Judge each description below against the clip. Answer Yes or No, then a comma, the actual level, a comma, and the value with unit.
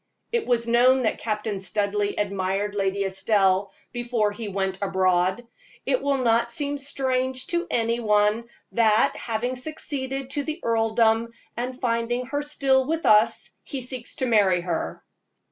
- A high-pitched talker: Yes, high, 230 Hz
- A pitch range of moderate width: Yes, average, 4.0 semitones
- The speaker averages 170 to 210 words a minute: No, average, 145 wpm